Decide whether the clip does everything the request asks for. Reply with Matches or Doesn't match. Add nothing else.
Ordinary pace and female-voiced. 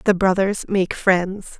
Matches